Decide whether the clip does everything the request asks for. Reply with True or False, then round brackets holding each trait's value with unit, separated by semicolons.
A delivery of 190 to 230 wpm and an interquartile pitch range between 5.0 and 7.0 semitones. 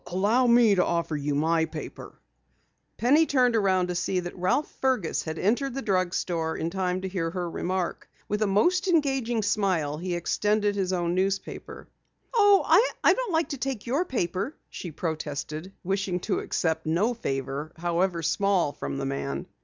False (170 wpm; 5.6 semitones)